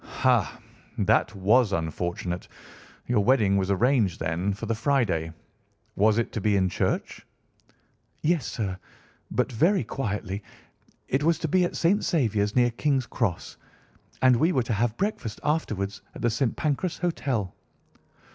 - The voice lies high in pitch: No, low, 115 Hz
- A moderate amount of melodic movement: No, wide, 5.8 semitones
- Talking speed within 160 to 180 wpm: No, average, 145 wpm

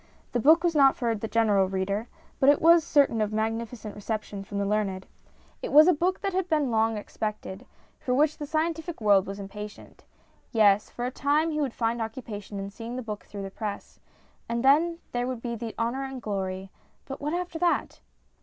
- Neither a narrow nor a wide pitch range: No, wide, 5.7 semitones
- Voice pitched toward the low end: No, high, 230 Hz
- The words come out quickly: Yes, fast, 210 wpm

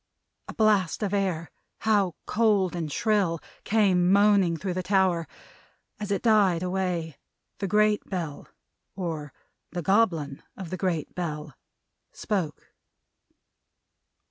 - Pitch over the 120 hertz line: Yes, medium, 185 Hz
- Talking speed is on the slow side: Yes, slow, 115 wpm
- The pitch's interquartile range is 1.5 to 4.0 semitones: Yes, average, 3.5 semitones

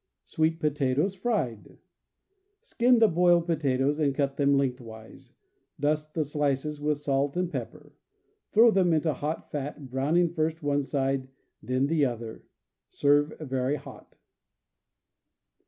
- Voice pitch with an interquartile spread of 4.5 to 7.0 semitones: No, average, 3.3 semitones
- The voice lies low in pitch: No, medium, 145 Hz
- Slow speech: Yes, slow, 130 wpm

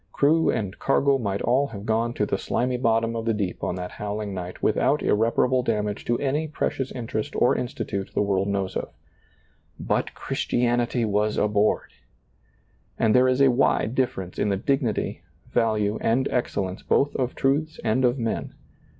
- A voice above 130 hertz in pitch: No, low, 115 Hz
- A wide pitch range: No, average, 3.7 semitones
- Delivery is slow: No, average, 165 wpm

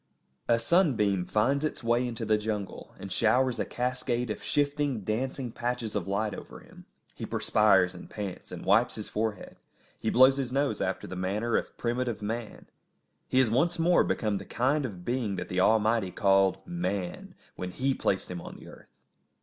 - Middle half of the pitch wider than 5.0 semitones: No, average, 4.1 semitones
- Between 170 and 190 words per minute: Yes, average, 180 wpm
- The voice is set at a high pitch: No, low, 115 Hz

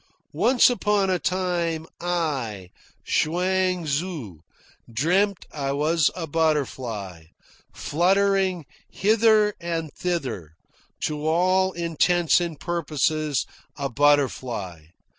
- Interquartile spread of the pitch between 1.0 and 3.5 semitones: No, average, 4.6 semitones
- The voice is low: No, medium, 165 Hz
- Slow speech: Yes, slow, 90 wpm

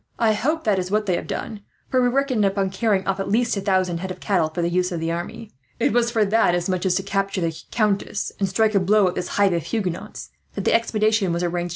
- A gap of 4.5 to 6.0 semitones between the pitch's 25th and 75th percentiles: No, average, 3.3 semitones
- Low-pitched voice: No, high, 195 Hz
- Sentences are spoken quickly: Yes, fast, 265 wpm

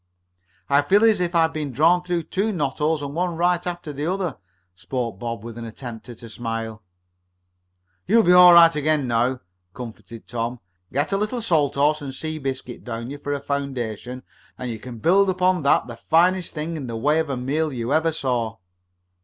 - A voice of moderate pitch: Yes, medium, 145 Hz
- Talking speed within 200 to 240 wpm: Yes, fast, 205 wpm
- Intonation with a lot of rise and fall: Yes, wide, 5.7 semitones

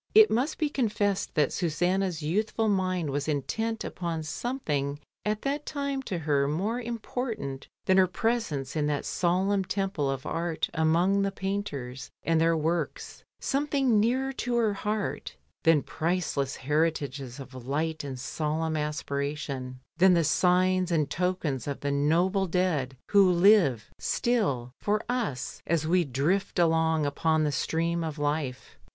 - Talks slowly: No, average, 145 wpm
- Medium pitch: Yes, medium, 170 Hz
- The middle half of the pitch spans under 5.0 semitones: No, wide, 5.4 semitones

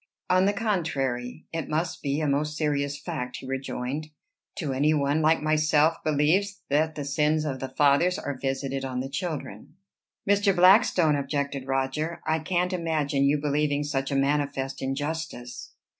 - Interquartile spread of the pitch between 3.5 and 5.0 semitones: No, narrow, 2.6 semitones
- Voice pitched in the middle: Yes, medium, 150 Hz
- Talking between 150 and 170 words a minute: Yes, average, 160 wpm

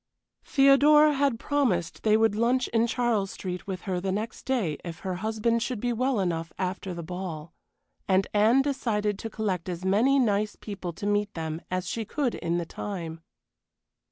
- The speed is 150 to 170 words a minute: No, average, 180 wpm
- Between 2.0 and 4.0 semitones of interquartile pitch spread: No, average, 4.7 semitones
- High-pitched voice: Yes, high, 205 Hz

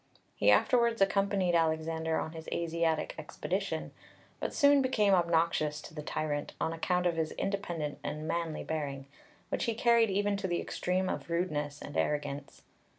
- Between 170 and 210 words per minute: No, average, 155 wpm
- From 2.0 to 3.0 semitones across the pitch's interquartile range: No, average, 4.1 semitones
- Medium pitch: Yes, medium, 165 Hz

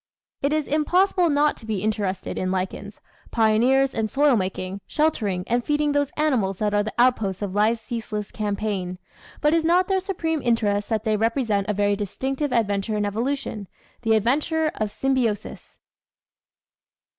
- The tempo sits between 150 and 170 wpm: Yes, average, 155 wpm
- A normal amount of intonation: No, wide, 5.7 semitones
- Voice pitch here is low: No, high, 225 Hz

